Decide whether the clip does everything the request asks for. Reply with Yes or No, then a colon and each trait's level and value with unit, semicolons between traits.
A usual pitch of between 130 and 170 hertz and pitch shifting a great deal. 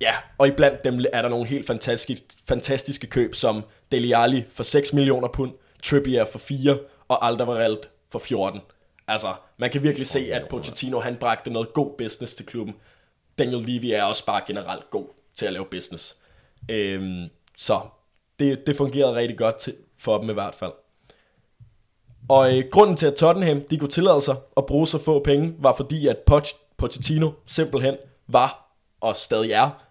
No: low, 135 Hz; average, 3.6 semitones